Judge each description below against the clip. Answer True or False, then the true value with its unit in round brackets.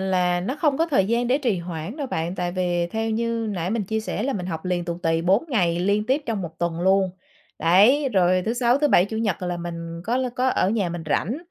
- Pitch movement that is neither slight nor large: True (5.0 semitones)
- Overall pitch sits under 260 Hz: True (190 Hz)